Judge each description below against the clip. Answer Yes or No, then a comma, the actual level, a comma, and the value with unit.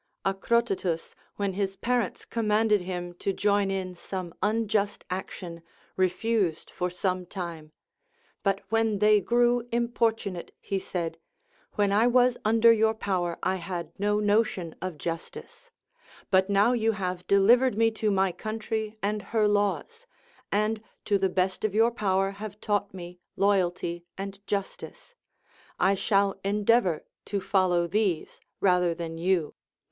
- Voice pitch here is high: Yes, high, 200 Hz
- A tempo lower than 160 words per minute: Yes, average, 140 wpm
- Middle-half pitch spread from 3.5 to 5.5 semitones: No, average, 3.0 semitones